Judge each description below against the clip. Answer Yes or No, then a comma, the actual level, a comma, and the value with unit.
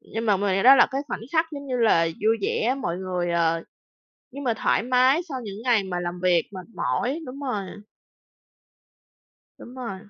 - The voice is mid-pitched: No, high, 225 Hz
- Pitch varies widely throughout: Yes, wide, 5.7 semitones